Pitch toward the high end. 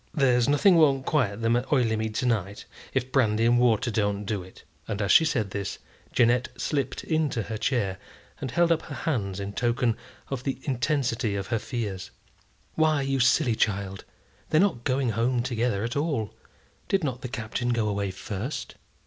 No: low, 120 Hz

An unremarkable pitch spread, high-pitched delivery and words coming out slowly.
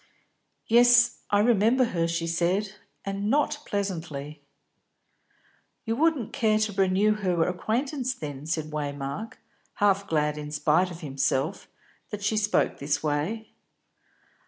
No: wide, 6.0 semitones; high, 195 Hz; slow, 130 wpm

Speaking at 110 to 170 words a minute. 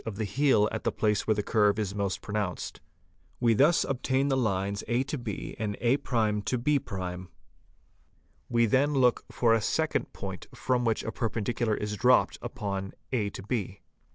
Yes: average, 165 wpm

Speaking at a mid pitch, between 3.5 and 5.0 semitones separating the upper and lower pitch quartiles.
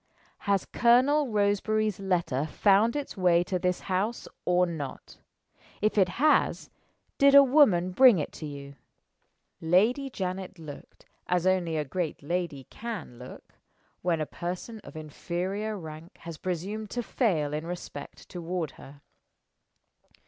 Yes: medium, 180 Hz; average, 4.7 semitones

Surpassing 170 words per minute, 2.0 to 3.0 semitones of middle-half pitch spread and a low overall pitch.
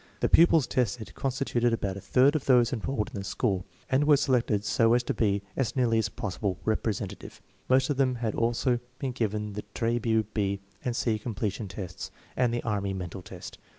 No: average, 190 wpm; average, 3.7 semitones; low, 115 Hz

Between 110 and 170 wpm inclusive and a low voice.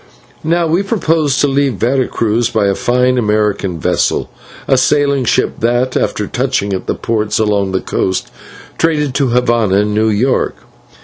Yes: average, 165 wpm; low, 120 Hz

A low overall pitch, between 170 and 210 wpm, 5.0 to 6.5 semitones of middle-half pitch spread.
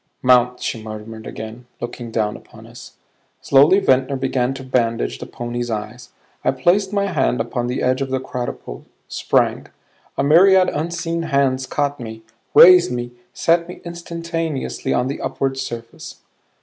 No: low, 130 Hz; average, 150 wpm; wide, 5.5 semitones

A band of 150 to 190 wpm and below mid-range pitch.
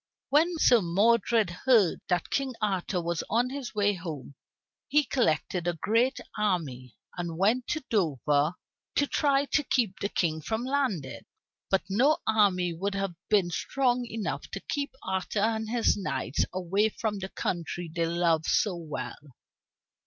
No: average, 155 wpm; high, 200 Hz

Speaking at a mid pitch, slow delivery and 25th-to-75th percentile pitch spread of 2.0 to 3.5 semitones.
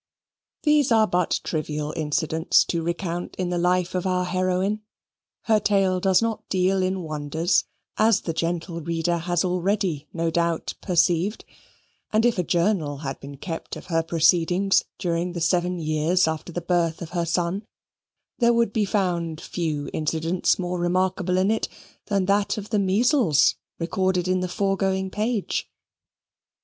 No: medium, 180 Hz; average, 155 wpm; narrow, 2.6 semitones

